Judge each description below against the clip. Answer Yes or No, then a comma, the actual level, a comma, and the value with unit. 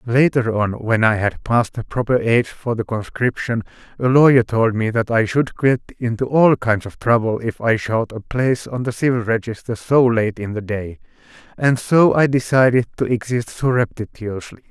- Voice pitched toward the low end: Yes, low, 120 Hz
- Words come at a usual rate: Yes, average, 190 wpm